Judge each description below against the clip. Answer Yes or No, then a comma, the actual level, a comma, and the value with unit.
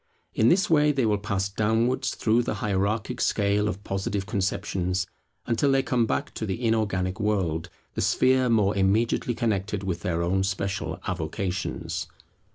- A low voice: Yes, low, 100 Hz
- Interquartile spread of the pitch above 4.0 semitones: No, average, 3.2 semitones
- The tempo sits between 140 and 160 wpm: Yes, average, 155 wpm